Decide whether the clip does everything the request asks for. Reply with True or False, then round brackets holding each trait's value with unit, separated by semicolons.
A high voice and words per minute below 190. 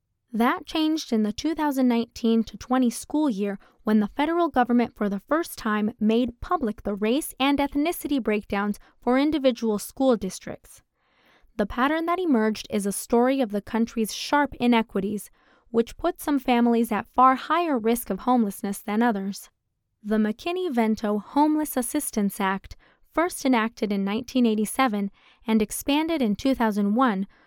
True (235 Hz; 140 wpm)